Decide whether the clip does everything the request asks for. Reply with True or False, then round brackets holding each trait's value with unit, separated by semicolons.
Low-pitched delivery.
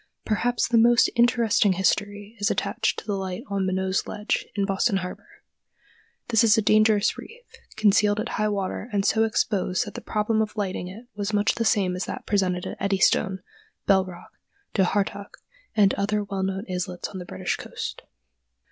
False (205 Hz)